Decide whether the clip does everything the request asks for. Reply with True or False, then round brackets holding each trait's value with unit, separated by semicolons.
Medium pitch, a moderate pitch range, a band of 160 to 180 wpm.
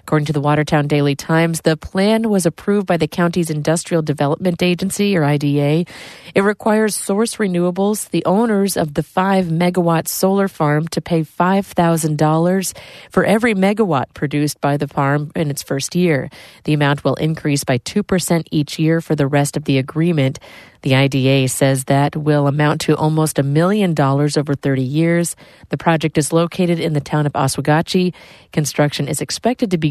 True (160 Hz; 3.4 semitones; 175 wpm)